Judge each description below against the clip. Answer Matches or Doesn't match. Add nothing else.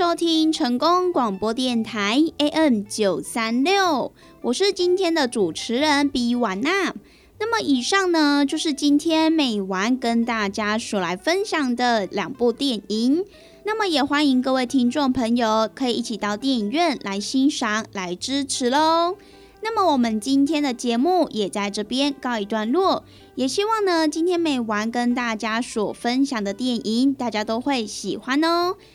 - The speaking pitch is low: Doesn't match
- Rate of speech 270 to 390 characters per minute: Doesn't match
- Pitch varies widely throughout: Matches